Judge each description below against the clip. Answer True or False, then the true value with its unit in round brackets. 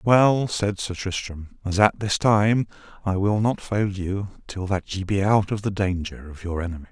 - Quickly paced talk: True (210 wpm)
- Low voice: True (100 Hz)